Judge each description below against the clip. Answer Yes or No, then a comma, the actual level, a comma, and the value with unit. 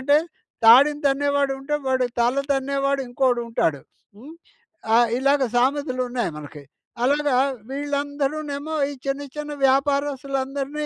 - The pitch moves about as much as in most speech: No, narrow, 1.8 semitones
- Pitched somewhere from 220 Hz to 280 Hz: Yes, very high, 275 Hz